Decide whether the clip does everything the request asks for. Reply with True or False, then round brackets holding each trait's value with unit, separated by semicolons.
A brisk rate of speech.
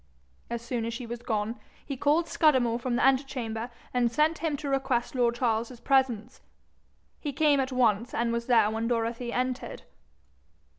False (165 wpm)